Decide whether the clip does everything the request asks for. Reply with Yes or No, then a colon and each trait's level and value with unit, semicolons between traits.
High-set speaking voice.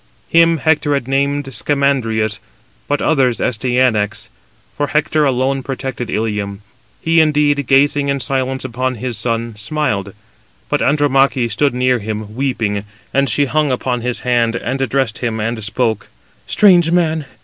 No: low, 130 Hz